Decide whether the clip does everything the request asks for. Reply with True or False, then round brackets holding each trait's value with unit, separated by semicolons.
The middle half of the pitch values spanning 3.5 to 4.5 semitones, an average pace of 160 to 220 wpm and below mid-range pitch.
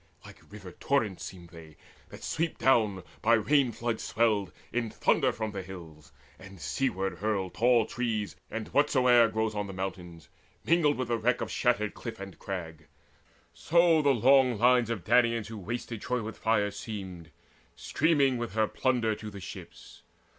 True (4.1 semitones; 170 wpm; 110 Hz)